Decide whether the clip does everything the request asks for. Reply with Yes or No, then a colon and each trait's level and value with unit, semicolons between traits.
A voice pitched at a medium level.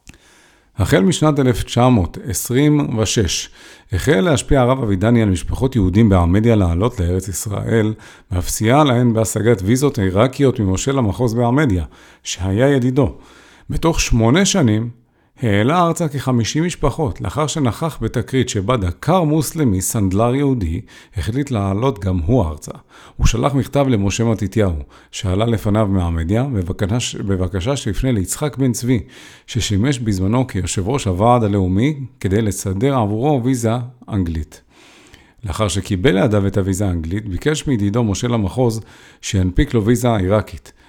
No: low, 115 Hz